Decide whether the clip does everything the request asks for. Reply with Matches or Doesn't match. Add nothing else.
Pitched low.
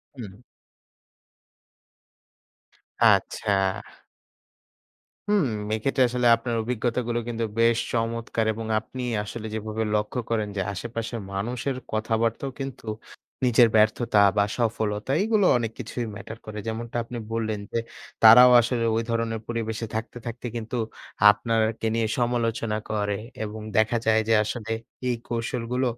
Matches